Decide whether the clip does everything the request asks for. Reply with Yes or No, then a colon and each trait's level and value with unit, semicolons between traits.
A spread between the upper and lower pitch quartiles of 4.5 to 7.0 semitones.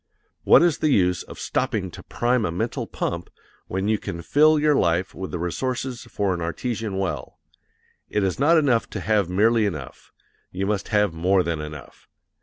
Yes: average, 5.3 semitones